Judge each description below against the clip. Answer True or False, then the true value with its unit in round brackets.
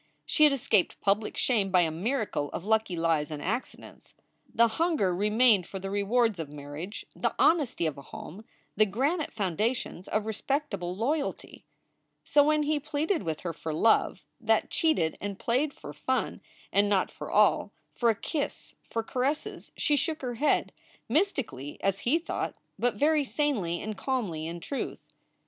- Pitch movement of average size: False (7.5 semitones)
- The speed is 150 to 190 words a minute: True (165 wpm)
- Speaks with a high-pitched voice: True (220 Hz)